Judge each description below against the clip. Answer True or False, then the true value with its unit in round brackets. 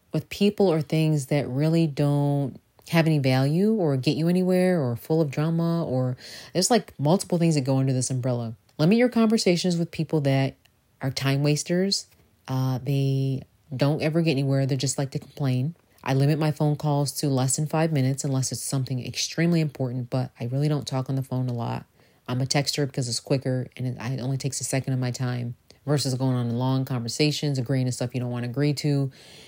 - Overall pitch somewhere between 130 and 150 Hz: True (140 Hz)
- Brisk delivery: True (210 wpm)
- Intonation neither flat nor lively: True (3.3 semitones)